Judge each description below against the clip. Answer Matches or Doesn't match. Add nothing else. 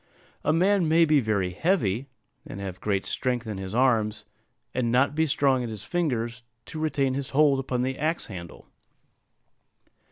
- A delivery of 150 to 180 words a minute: Matches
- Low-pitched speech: Matches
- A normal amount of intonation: Doesn't match